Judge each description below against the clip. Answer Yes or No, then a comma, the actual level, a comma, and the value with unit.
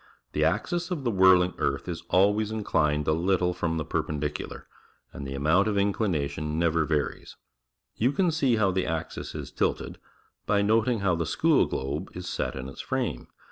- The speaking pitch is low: Yes, very low, 90 Hz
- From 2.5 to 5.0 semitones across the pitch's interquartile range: No, wide, 5.4 semitones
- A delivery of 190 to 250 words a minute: Yes, average, 195 wpm